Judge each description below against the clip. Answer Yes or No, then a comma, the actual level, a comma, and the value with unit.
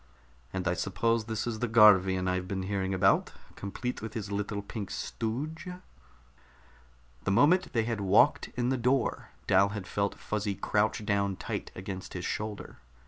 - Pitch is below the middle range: Yes, low, 105 Hz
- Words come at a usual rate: Yes, average, 160 wpm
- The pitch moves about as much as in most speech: Yes, average, 3.1 semitones